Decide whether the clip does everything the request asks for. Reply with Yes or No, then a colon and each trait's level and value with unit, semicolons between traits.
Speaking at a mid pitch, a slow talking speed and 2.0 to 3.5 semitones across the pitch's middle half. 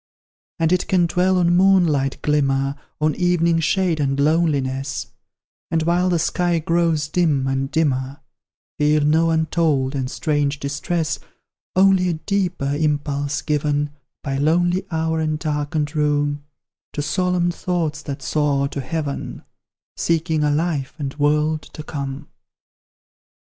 Yes: medium, 155 Hz; slow, 130 wpm; average, 2.9 semitones